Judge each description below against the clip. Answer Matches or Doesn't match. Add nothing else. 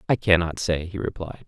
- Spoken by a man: Matches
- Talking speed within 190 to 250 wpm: Matches